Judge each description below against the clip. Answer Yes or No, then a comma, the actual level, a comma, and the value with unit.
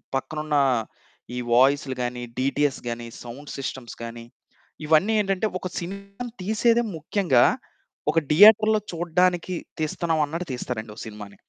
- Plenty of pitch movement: Yes, wide, 6.5 semitones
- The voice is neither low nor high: Yes, medium, 155 Hz